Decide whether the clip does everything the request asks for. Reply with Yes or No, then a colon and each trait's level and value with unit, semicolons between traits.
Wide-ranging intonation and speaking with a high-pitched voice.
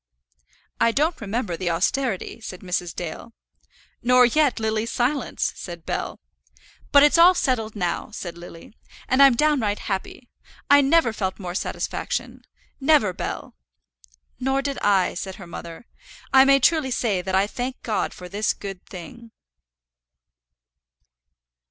Yes: wide, 6.2 semitones; high, 225 Hz